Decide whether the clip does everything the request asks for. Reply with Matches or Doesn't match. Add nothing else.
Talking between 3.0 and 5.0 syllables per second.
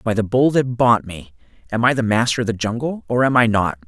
Doesn't match